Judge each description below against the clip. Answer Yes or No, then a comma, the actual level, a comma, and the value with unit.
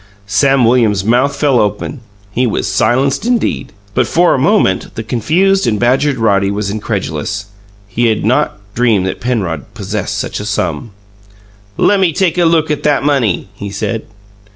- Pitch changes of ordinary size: No, wide, 5.8 semitones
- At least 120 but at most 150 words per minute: No, average, 160 wpm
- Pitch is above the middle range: No, low, 120 Hz